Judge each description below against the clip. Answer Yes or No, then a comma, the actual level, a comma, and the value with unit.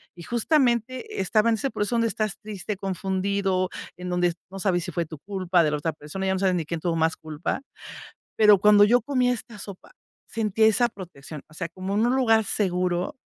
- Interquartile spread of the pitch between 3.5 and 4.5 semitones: Yes, average, 3.8 semitones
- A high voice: Yes, high, 195 Hz